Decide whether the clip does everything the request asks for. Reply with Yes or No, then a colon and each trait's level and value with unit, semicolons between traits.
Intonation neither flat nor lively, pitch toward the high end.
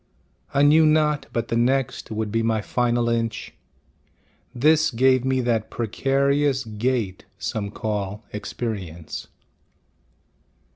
No: average, 3.6 semitones; low, 120 Hz